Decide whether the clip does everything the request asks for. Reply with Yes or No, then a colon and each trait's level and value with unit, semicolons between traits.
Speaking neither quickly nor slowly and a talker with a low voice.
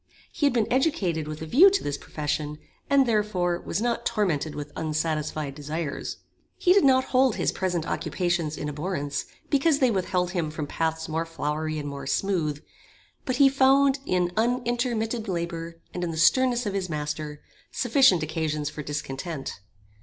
No: average, 165 wpm; medium, 170 Hz